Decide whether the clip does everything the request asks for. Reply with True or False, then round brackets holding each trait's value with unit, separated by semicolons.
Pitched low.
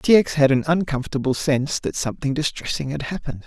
False (145 Hz)